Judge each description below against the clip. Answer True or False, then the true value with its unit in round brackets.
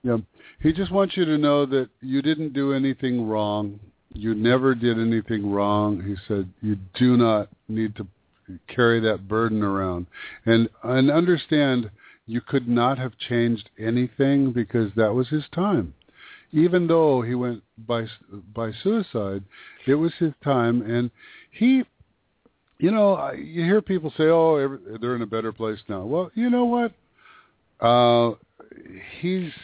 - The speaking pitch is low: True (120 Hz)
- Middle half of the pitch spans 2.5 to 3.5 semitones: False (5.5 semitones)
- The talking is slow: False (155 wpm)